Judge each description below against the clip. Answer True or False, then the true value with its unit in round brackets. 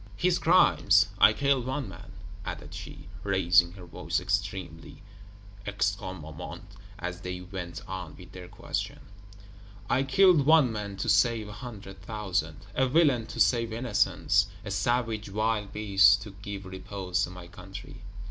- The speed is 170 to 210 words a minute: False (145 wpm)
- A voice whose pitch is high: False (100 Hz)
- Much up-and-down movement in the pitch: False (4.1 semitones)